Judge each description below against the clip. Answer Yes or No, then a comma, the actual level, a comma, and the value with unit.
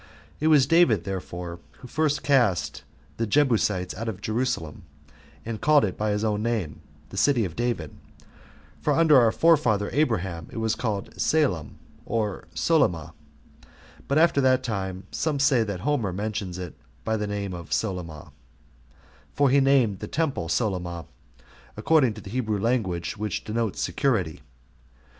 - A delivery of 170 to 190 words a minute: No, average, 150 wpm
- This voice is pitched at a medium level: No, low, 110 Hz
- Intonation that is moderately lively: No, wide, 6.0 semitones